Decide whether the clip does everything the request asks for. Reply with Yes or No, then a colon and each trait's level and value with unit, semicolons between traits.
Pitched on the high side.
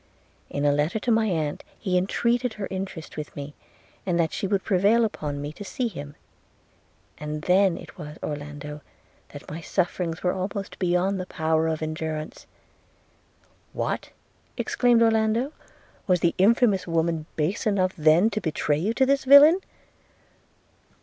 No: medium, 180 Hz